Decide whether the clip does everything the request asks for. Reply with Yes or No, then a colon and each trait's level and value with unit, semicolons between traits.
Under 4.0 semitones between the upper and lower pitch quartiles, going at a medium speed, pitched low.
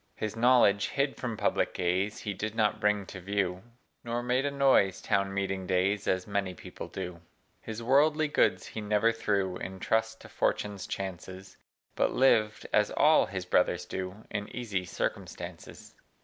Yes: average, 3.3 semitones; average, 165 wpm; low, 105 Hz